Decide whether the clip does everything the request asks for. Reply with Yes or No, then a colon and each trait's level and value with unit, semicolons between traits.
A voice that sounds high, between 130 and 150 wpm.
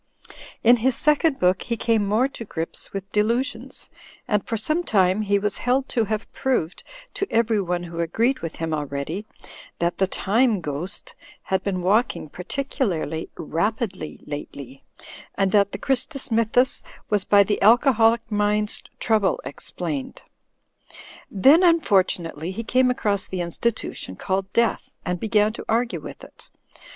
Yes: high, 210 Hz; average, 145 wpm